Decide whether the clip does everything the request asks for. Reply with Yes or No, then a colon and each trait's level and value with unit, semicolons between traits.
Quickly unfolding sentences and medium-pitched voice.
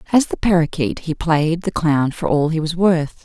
Yes: fast, 220 wpm; medium, 165 Hz